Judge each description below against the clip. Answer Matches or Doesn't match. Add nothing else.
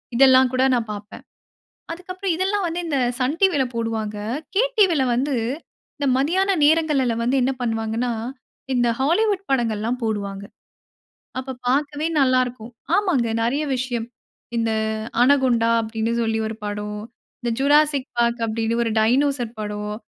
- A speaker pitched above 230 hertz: Matches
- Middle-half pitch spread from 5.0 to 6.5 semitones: Doesn't match